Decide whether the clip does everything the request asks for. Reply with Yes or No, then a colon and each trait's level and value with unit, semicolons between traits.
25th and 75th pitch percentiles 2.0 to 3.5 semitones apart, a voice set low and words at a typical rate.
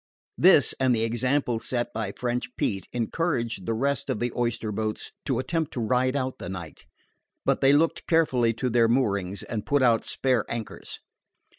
Yes: average, 2.8 semitones; low, 120 Hz; average, 175 wpm